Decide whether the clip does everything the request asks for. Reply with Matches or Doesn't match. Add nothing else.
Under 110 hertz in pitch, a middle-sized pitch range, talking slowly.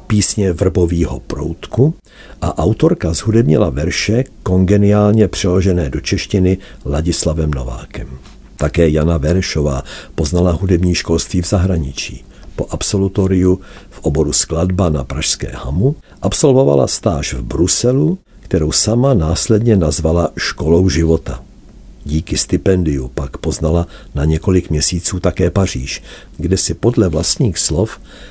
Matches